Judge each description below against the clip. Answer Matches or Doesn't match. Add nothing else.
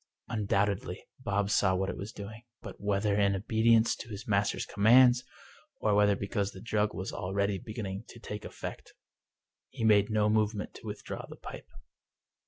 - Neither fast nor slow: Matches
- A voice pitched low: Matches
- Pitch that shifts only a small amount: Matches